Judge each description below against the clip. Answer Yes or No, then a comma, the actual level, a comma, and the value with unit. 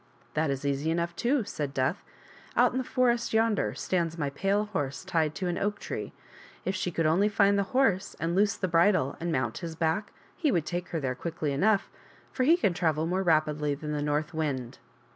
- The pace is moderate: No, fast, 220 wpm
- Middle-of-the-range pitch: Yes, medium, 170 Hz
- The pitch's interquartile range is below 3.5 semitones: No, average, 4.9 semitones